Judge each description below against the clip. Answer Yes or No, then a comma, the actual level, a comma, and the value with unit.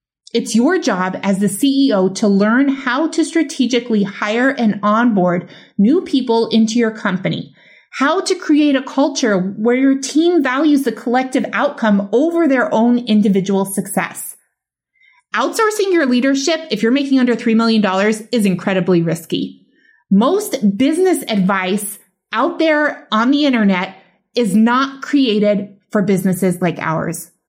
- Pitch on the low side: No, high, 230 Hz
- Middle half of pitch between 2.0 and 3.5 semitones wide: No, wide, 5.6 semitones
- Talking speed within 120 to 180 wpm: Yes, average, 140 wpm